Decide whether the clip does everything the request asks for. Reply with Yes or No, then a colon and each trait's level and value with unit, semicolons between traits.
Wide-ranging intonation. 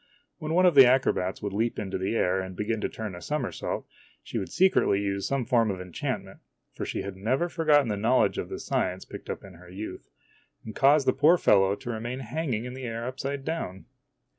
Yes: wide, 5.7 semitones